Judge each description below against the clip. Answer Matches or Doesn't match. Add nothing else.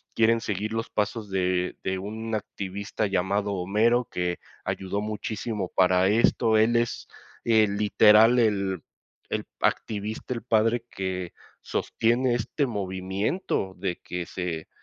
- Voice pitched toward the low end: Matches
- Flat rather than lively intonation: Doesn't match